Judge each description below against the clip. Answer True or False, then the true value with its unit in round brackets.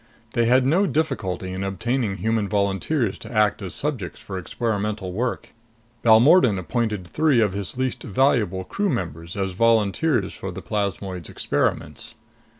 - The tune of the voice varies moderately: True (4.5 semitones)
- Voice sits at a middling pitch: False (105 Hz)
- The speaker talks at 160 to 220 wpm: False (145 wpm)